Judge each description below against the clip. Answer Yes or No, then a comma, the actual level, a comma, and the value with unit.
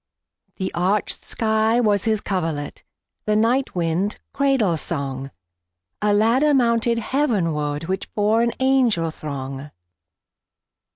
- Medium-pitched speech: No, high, 205 Hz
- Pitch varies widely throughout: Yes, wide, 7.3 semitones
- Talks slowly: Yes, slow, 95 wpm